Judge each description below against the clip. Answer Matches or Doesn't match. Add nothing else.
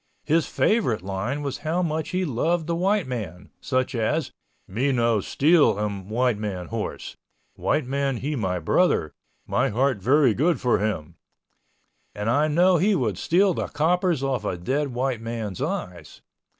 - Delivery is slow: Doesn't match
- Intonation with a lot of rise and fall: Matches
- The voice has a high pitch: Doesn't match